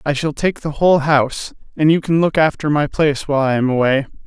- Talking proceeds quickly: Yes, fast, 240 wpm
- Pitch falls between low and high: Yes, medium, 145 Hz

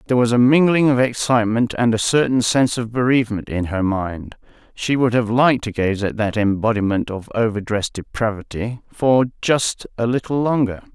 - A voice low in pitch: Yes, low, 115 Hz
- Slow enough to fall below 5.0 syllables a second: No, 5.4 syllables/s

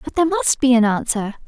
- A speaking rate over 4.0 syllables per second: Yes, 6.3 syllables/s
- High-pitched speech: Yes, high, 245 Hz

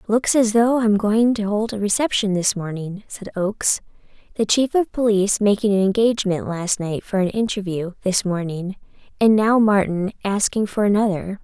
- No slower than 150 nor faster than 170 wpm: No, average, 180 wpm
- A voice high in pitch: Yes, high, 205 Hz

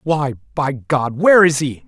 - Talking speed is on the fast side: No, average, 195 wpm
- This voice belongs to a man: Yes, male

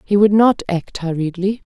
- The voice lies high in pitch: Yes, high, 195 Hz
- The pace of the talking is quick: No, average, 175 wpm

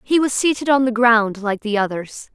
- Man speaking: No, female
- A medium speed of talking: No, fast, 230 wpm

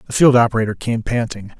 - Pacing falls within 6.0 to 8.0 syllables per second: Yes, 6.5 syllables/s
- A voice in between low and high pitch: No, low, 115 Hz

